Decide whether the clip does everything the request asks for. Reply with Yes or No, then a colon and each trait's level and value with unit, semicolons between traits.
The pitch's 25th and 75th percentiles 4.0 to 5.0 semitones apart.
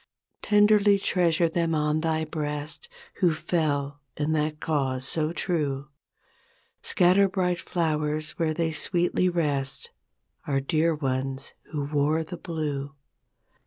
No: average, 2.9 semitones